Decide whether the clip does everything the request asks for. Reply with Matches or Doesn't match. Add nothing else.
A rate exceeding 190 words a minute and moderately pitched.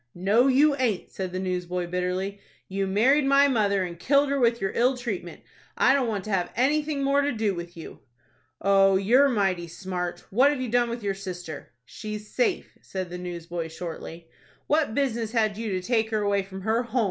Doesn't match